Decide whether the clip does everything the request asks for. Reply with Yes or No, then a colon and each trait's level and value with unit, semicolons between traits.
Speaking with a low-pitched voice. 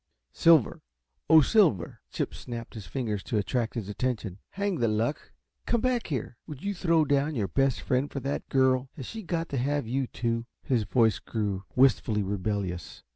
Yes: low, 125 Hz